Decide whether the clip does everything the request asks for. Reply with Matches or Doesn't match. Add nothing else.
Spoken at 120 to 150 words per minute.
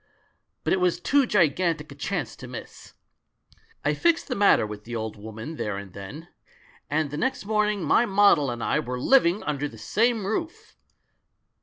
Doesn't match